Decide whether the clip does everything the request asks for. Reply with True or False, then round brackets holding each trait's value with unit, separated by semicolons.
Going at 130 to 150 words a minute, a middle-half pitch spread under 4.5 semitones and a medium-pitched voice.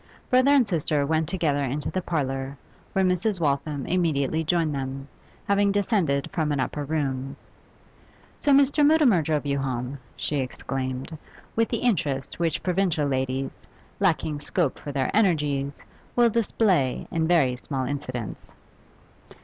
False (140 wpm; 5.3 semitones; 150 Hz)